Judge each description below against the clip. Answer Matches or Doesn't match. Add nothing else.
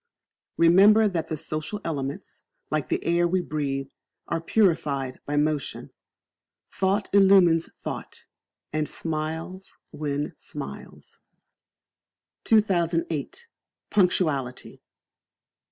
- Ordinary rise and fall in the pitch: Matches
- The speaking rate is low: Matches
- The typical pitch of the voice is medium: Matches